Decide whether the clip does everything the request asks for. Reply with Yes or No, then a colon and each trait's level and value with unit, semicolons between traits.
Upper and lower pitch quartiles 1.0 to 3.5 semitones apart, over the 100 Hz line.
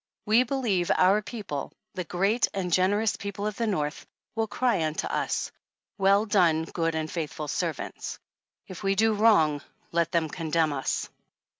No: average, 4.7 semitones; medium, 185 Hz